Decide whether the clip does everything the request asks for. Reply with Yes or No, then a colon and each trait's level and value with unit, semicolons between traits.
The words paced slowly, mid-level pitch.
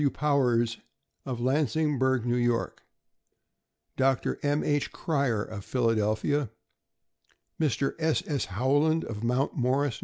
No: slow, 125 wpm; low, 130 Hz